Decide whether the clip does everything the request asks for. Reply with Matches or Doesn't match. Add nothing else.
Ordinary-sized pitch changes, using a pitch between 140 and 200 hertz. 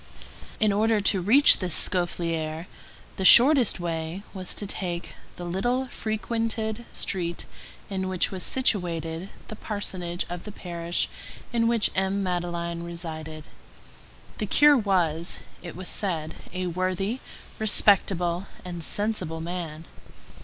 Matches